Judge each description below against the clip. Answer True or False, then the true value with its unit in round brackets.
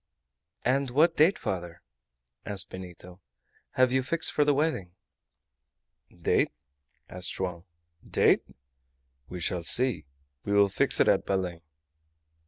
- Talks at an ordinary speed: False (120 wpm)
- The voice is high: False (100 Hz)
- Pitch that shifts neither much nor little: False (6.7 semitones)